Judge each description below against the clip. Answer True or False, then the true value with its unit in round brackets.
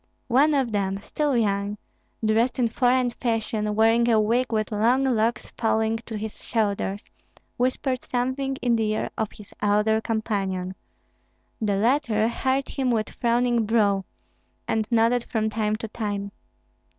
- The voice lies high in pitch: True (225 Hz)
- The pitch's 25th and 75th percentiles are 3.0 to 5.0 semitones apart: False (2.5 semitones)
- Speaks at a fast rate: False (145 wpm)